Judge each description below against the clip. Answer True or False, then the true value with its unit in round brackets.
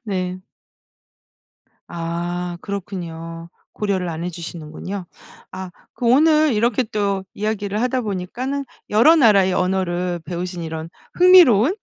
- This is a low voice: False (190 Hz)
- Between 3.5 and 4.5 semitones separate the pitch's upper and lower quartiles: True (4.1 semitones)